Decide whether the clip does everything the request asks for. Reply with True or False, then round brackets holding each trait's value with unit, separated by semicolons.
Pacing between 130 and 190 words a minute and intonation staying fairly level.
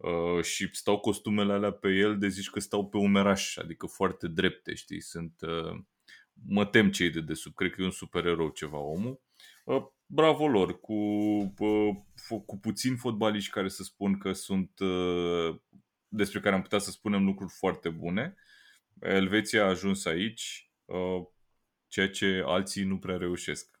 True (150 wpm; 2.3 semitones)